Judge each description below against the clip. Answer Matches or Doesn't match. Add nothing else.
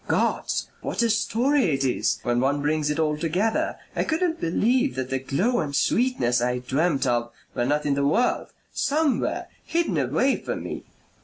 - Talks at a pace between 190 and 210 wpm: Doesn't match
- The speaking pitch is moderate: Matches